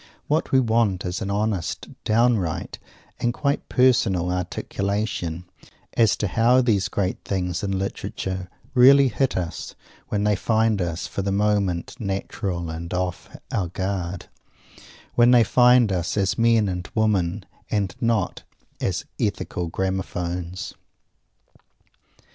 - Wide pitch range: No, average, 3.9 semitones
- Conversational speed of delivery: No, slow, 125 wpm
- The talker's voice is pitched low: Yes, low, 100 Hz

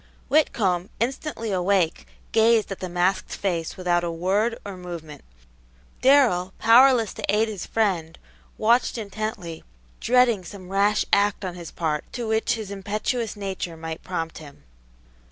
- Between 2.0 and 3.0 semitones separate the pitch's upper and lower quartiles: No, average, 4.1 semitones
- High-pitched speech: Yes, high, 195 Hz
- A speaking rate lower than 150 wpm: Yes, average, 140 wpm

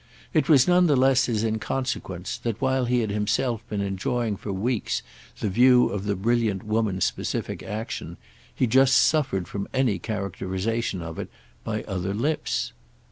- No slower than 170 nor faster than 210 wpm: No, average, 160 wpm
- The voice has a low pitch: Yes, low, 110 Hz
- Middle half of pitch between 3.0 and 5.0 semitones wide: Yes, average, 4.4 semitones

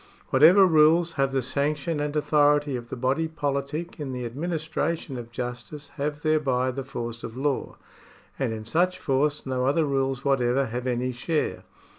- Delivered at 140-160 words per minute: No, average, 170 wpm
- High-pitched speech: No, medium, 140 Hz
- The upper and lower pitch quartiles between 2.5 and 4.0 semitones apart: Yes, average, 3.2 semitones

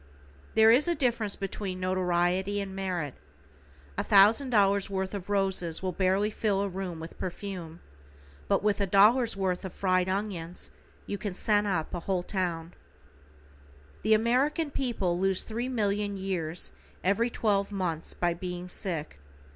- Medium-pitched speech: No, high, 195 Hz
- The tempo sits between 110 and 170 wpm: Yes, average, 150 wpm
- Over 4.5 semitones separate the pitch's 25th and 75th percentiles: No, narrow, 2.6 semitones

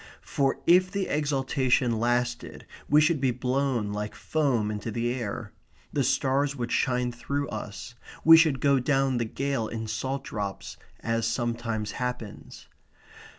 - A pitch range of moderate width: Yes, average, 3.3 semitones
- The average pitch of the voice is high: No, low, 125 Hz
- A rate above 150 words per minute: No, average, 145 wpm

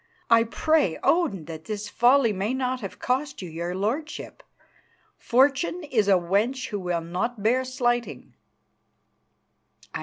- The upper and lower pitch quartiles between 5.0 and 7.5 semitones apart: Yes, average, 5.3 semitones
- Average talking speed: No, slow, 130 wpm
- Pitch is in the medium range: No, high, 230 Hz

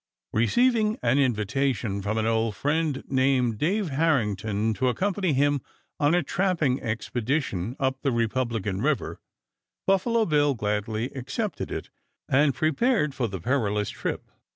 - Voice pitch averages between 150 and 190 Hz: No, low, 130 Hz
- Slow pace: Yes, slow, 130 wpm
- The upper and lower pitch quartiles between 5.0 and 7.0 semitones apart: Yes, wide, 5.5 semitones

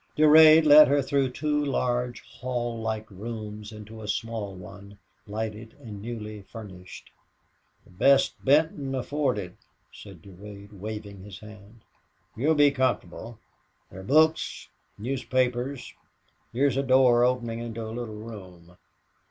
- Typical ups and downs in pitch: Yes, average, 4.1 semitones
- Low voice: Yes, low, 115 Hz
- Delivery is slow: Yes, slow, 125 wpm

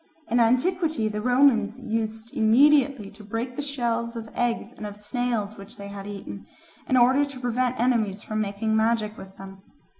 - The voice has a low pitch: No, high, 230 Hz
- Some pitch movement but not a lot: Yes, average, 3.0 semitones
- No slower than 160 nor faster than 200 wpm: Yes, average, 175 wpm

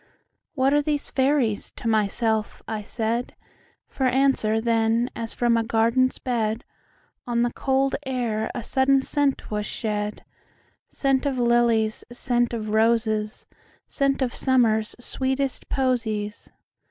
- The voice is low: No, high, 235 Hz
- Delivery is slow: Yes, slow, 115 wpm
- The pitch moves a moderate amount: Yes, average, 3.1 semitones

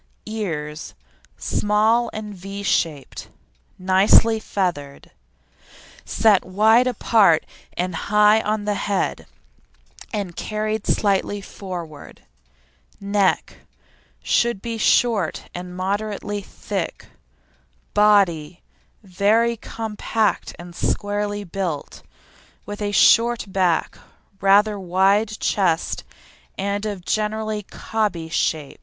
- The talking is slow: Yes, slow, 90 wpm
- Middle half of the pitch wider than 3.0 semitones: No, average, 2.7 semitones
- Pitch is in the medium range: No, high, 205 Hz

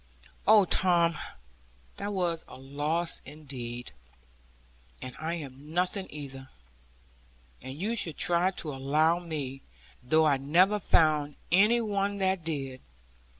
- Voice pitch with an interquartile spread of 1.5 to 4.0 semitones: No, average, 4.8 semitones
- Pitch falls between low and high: Yes, medium, 160 Hz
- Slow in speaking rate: Yes, slow, 125 wpm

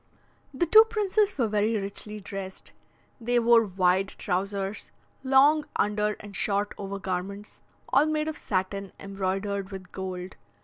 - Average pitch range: Yes, average, 3.8 semitones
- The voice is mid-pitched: No, high, 205 Hz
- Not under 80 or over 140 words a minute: Yes, slow, 135 wpm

